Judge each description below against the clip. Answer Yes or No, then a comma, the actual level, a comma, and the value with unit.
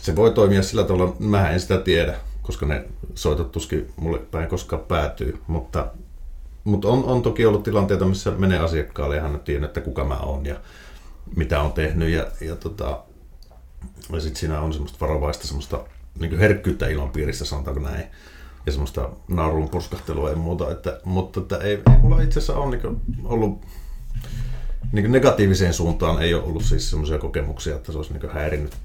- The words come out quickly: Yes, fast, 180 wpm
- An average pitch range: Yes, average, 4.7 semitones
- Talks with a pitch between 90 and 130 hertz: No, very low, 80 Hz